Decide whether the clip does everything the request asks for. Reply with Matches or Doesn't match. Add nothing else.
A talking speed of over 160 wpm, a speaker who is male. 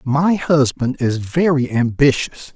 Doesn't match